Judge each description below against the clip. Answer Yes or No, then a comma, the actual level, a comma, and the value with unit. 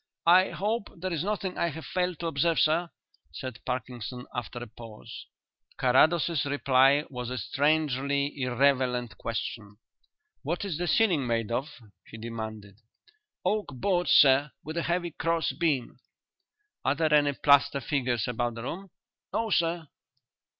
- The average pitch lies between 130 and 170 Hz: Yes, medium, 140 Hz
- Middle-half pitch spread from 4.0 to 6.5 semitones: Yes, wide, 5.4 semitones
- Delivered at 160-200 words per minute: No, average, 145 wpm